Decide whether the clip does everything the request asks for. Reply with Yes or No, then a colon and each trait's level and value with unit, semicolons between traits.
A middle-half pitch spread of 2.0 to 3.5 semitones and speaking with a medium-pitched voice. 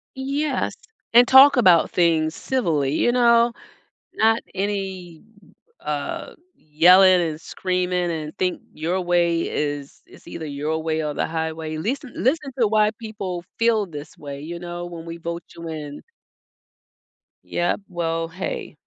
No: average, 4.9 semitones; medium, 175 Hz